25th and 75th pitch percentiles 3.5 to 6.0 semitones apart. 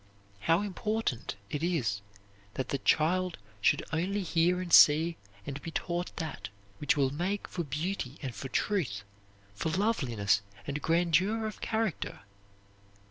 Yes: average, 4.9 semitones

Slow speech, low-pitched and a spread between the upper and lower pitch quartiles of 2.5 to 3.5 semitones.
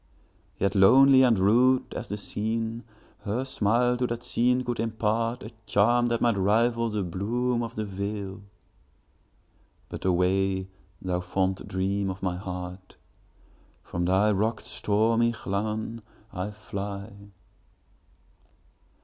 Yes: slow, 110 wpm; low, 105 Hz; average, 3.2 semitones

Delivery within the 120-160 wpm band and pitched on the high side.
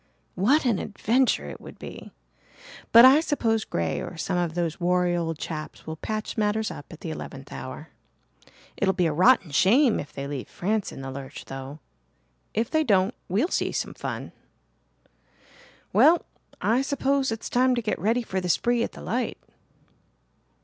No: average, 170 wpm; high, 195 Hz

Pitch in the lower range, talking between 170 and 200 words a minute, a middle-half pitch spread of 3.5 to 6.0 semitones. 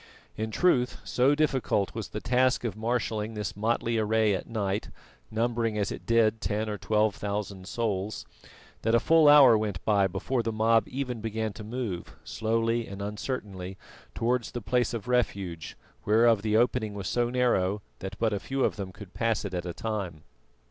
No: low, 110 Hz; average, 175 wpm; narrow, 2.6 semitones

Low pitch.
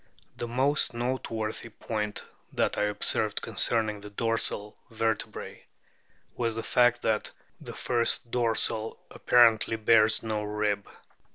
Yes: low, 110 Hz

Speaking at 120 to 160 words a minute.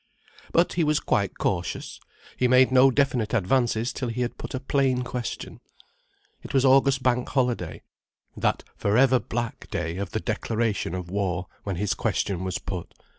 No: average, 170 wpm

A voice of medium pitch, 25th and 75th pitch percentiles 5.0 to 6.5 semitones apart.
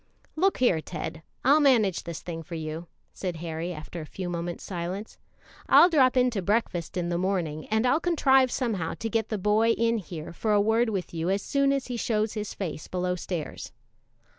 No: high, 195 Hz; average, 5.3 semitones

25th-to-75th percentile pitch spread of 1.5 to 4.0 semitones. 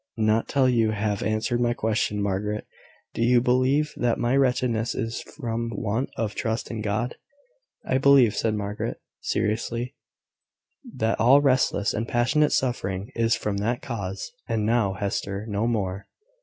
Yes: average, 2.7 semitones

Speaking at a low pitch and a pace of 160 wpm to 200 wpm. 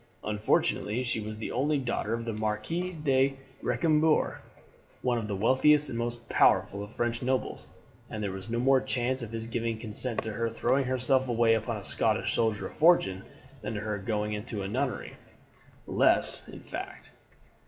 Yes: low, 115 Hz; average, 180 wpm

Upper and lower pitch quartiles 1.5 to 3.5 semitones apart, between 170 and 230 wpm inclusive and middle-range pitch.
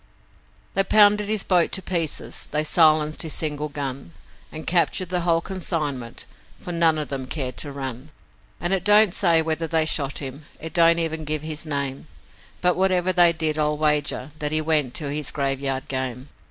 Yes: average, 3.2 semitones; average, 180 wpm; medium, 155 Hz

